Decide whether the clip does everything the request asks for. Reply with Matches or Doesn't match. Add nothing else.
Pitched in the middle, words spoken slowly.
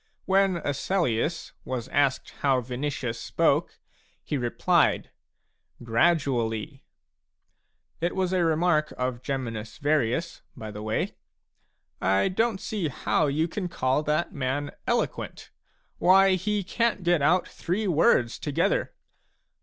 Matches